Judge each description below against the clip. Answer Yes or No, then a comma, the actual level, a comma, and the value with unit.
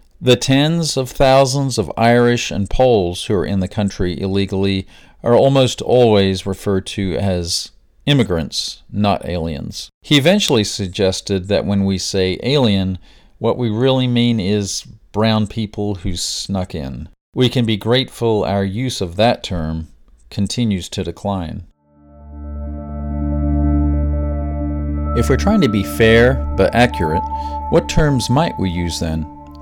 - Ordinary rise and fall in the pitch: No, wide, 6.3 semitones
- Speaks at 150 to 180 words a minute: No, slow, 135 wpm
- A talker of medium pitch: No, low, 100 Hz